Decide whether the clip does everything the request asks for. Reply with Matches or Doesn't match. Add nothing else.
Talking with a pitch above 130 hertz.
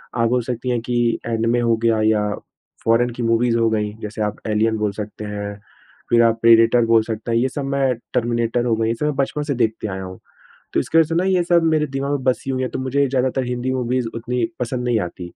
Doesn't match